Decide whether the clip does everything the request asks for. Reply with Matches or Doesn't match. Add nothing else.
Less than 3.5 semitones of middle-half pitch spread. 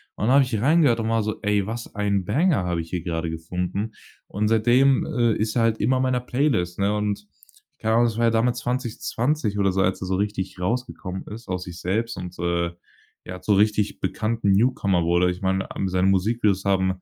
Doesn't match